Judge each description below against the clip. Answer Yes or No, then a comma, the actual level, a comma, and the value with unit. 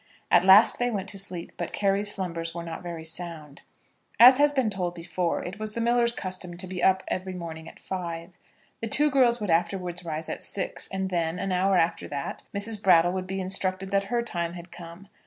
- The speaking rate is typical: No, fast, 210 wpm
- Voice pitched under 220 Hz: Yes, medium, 185 Hz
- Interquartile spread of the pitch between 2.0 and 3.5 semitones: Yes, average, 2.9 semitones